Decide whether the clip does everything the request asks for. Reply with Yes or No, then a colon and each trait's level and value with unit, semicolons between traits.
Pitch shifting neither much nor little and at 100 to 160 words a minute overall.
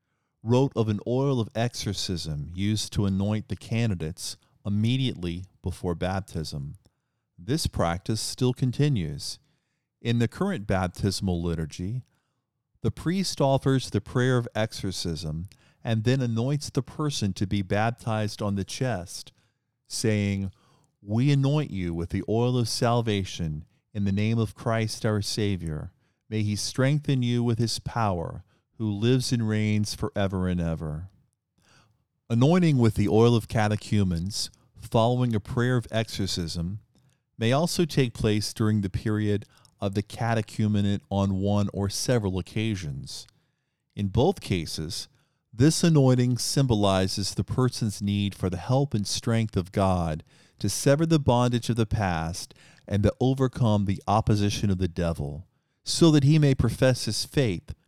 Yes: average, 4.1 semitones; average, 140 wpm